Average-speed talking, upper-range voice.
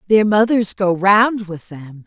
Yes: average, 175 wpm; high, 195 Hz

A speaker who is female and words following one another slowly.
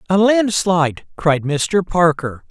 No: male; slow, 120 wpm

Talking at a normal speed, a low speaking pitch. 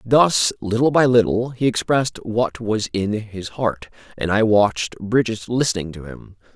Yes: average, 165 wpm; low, 110 Hz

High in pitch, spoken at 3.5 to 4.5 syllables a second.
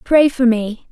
Yes: high, 245 Hz; 4.0 syllables/s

